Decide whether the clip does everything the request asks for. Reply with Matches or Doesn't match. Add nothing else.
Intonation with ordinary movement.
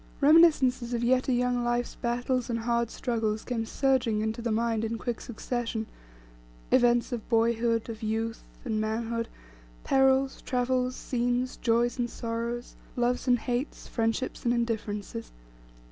Doesn't match